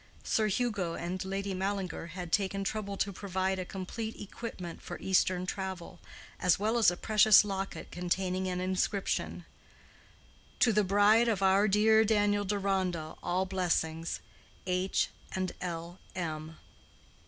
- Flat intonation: Yes, narrow, 2.1 semitones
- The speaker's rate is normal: No, slow, 130 wpm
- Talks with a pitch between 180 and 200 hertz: Yes, high, 190 Hz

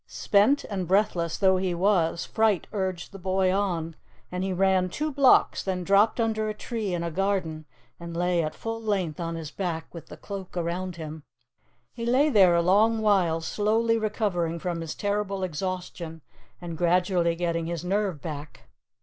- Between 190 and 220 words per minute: No, average, 175 wpm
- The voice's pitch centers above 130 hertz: Yes, medium, 185 Hz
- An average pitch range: Yes, average, 3.3 semitones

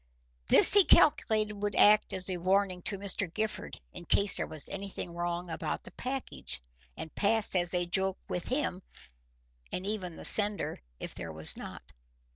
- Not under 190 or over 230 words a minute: No, average, 170 wpm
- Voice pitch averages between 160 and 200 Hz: Yes, high, 190 Hz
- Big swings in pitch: No, average, 3.1 semitones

